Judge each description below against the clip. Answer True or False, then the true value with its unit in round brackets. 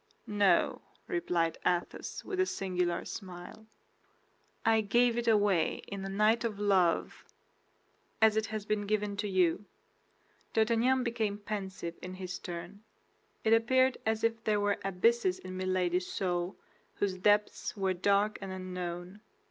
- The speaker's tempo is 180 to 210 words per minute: False (140 wpm)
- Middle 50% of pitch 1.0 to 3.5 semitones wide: True (3.0 semitones)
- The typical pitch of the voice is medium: False (200 Hz)